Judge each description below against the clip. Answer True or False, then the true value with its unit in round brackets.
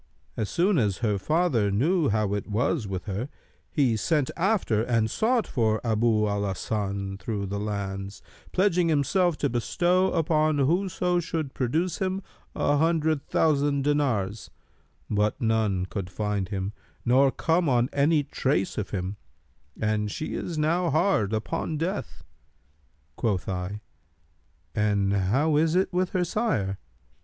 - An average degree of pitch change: False (8.0 semitones)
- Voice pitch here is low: True (125 Hz)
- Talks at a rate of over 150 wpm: False (140 wpm)